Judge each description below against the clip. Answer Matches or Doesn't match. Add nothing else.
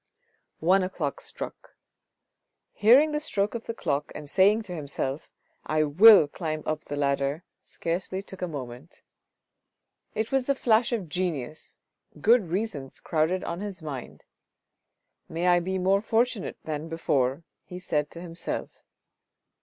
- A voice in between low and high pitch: Matches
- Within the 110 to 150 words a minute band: Matches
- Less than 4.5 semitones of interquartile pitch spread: Doesn't match